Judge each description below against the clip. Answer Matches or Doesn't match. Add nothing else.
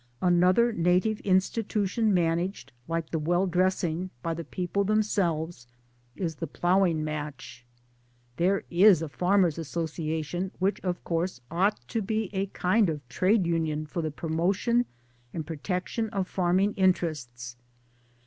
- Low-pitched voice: Doesn't match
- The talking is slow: Matches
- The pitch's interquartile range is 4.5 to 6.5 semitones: Doesn't match